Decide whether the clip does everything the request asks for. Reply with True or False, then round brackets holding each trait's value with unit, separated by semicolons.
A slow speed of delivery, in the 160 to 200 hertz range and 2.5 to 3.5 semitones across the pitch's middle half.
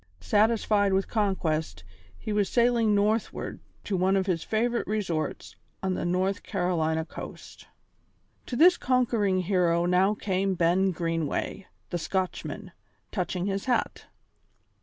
True (125 wpm; 190 Hz; 3.2 semitones)